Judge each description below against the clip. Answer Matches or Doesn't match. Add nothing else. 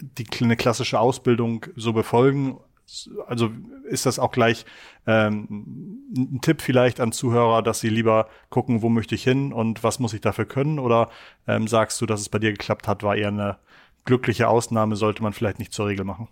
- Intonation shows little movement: Matches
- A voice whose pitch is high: Doesn't match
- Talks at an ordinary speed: Doesn't match